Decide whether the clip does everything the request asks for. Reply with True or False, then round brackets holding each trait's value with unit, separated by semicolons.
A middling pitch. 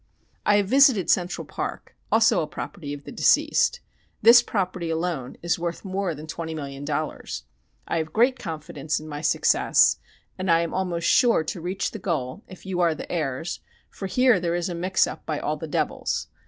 True (175 Hz)